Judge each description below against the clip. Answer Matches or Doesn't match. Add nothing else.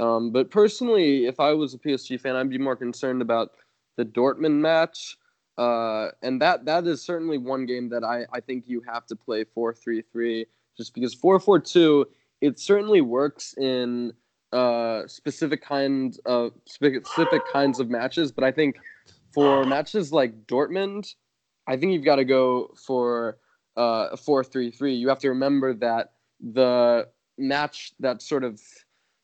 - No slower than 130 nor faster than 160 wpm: Matches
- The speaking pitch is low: Matches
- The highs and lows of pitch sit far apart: Doesn't match